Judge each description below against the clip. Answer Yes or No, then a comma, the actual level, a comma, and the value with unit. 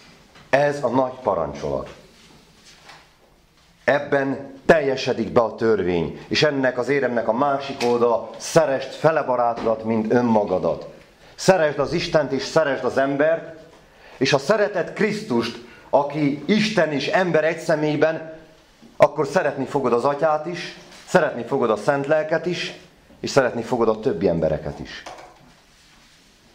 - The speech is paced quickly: No, average, 130 wpm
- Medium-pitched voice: Yes, medium, 145 Hz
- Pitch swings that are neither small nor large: Yes, average, 4.9 semitones